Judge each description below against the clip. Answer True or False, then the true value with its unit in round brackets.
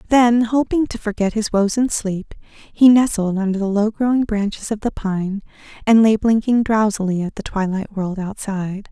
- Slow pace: False (180 wpm)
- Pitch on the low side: False (210 Hz)